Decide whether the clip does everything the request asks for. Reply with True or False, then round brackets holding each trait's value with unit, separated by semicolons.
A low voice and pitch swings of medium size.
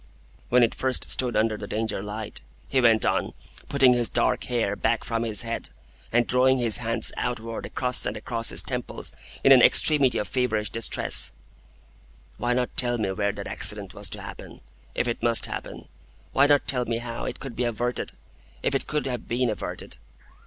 False (120 Hz; 2.1 semitones)